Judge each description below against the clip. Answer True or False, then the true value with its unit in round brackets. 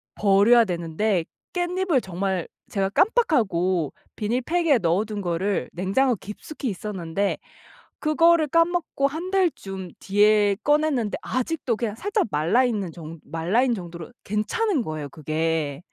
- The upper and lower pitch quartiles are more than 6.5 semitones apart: True (8.6 semitones)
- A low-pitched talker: False (210 Hz)